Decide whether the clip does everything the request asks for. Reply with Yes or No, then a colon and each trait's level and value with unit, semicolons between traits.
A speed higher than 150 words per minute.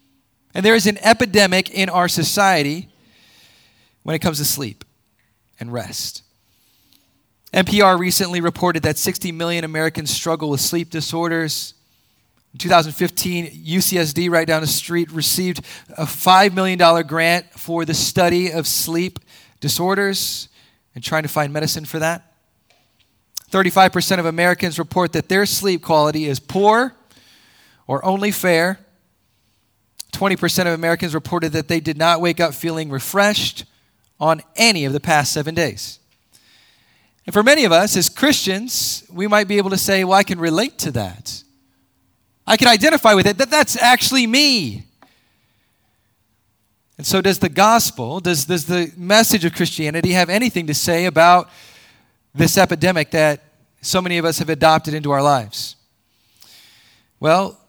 No: average, 145 wpm